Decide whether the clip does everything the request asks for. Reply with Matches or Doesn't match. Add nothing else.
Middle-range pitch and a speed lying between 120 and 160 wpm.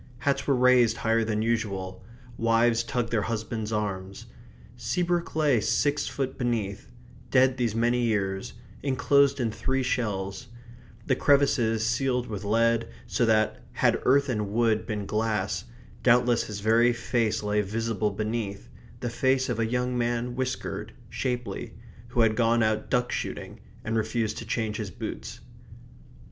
Doesn't match